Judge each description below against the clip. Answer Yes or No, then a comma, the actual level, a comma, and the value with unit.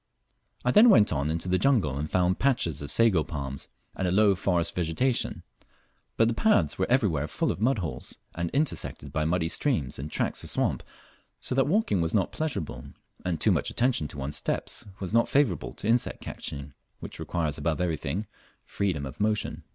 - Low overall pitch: Yes, very low, 90 Hz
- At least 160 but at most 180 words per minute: No, average, 190 wpm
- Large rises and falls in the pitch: Yes, wide, 6.9 semitones